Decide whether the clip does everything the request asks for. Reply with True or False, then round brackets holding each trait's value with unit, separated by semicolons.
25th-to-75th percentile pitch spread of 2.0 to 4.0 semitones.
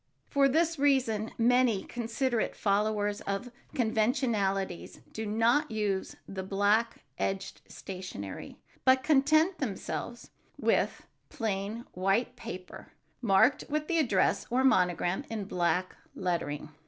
False (4.9 semitones)